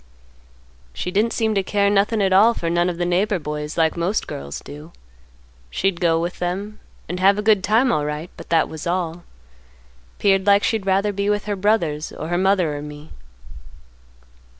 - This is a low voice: No, medium, 185 Hz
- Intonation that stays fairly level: No, average, 3.7 semitones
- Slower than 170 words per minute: No, average, 185 wpm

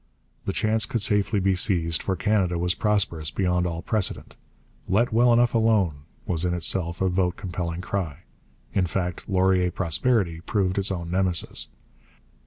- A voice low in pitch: Yes, very low, 95 Hz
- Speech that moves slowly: No, average, 155 wpm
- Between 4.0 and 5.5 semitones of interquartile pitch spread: No, average, 2.9 semitones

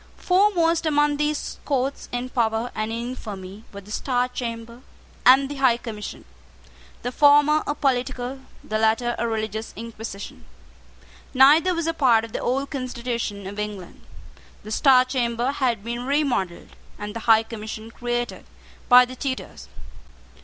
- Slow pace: No, average, 145 wpm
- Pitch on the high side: Yes, high, 245 Hz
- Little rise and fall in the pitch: No, average, 3.5 semitones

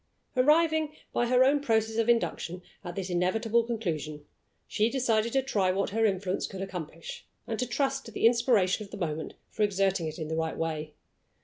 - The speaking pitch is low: No, high, 210 Hz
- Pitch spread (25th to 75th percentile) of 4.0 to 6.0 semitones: Yes, average, 4.9 semitones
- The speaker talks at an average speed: Yes, average, 190 wpm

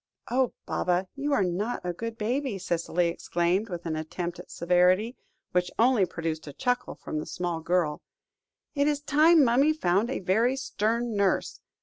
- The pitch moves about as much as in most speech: No, wide, 6.1 semitones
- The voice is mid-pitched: No, high, 195 Hz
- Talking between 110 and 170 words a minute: Yes, average, 165 wpm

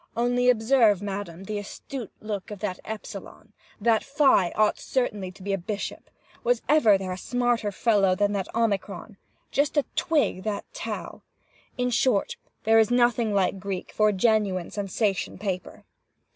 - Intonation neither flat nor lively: Yes, average, 3.5 semitones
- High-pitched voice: Yes, high, 210 Hz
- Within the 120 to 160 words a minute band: Yes, average, 155 wpm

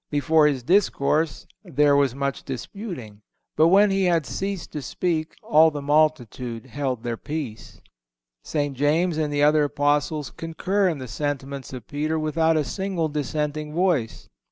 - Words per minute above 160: No, average, 155 wpm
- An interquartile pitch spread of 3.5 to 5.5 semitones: No, average, 2.7 semitones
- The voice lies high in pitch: No, medium, 150 Hz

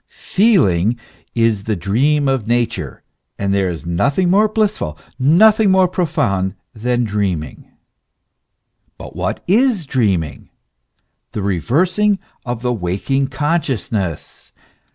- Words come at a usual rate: No, slow, 110 wpm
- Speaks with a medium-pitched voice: No, low, 120 Hz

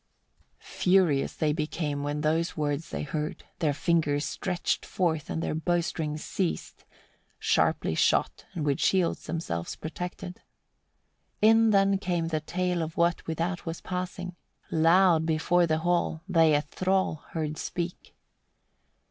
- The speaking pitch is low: No, medium, 165 Hz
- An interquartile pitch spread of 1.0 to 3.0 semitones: Yes, narrow, 2.6 semitones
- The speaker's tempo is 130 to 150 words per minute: Yes, average, 140 wpm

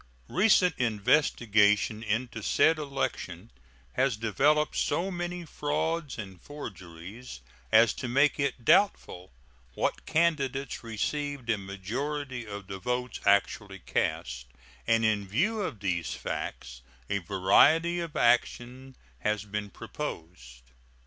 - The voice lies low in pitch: Yes, low, 115 Hz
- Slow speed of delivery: Yes, slow, 115 wpm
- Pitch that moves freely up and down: Yes, wide, 6.5 semitones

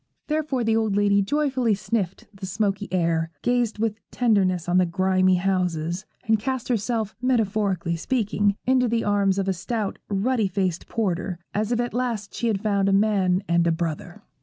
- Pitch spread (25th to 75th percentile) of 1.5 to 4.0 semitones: Yes, average, 3.4 semitones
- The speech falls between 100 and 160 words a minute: No, average, 175 wpm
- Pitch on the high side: Yes, high, 205 Hz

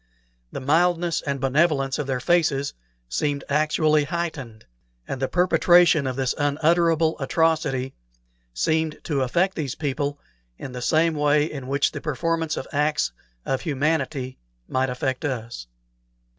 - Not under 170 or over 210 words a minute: No, slow, 135 wpm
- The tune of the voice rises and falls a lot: No, average, 3.4 semitones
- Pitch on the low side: No, medium, 145 Hz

